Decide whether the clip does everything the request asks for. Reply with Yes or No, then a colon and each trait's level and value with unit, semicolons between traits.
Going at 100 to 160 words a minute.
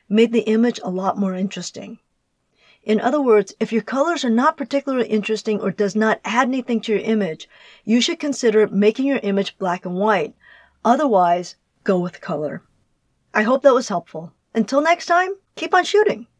No: average, 180 wpm